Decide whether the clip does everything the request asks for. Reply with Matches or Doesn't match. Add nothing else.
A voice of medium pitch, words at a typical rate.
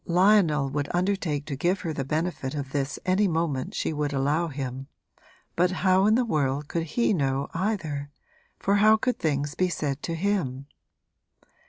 Matches